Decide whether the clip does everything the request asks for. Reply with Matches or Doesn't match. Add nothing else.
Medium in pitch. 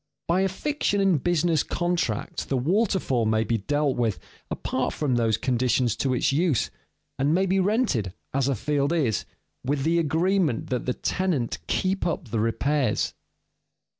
Matches